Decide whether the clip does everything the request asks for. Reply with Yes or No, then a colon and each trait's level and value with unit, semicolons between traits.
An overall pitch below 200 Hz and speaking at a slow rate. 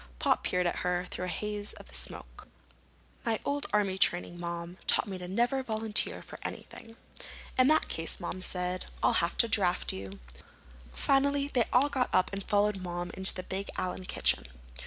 No: high, 190 Hz; average, 180 wpm